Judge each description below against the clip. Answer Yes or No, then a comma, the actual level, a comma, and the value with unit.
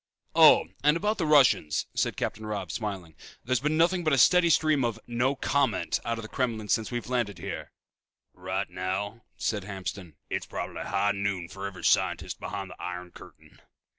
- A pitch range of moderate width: No, wide, 5.8 semitones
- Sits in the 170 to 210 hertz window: No, low, 110 Hz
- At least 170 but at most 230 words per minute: Yes, average, 180 wpm